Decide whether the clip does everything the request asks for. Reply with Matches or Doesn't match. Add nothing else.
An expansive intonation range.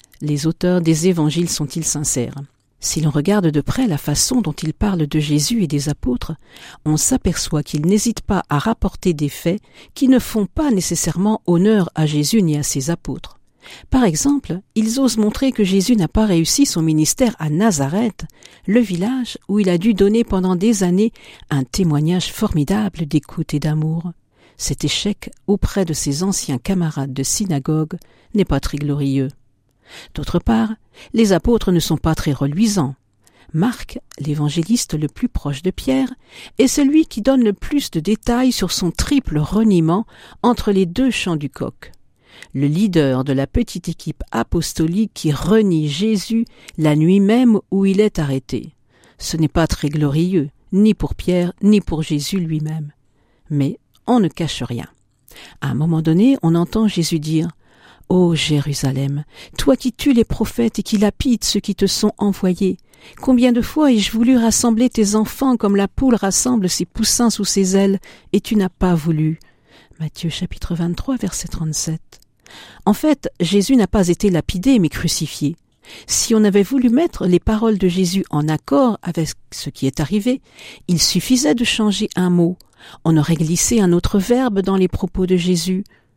Matches